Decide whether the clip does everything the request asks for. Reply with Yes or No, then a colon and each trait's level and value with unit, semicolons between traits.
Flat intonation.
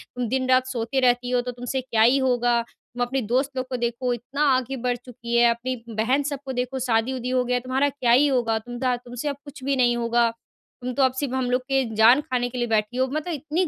Yes: narrow, 1.6 semitones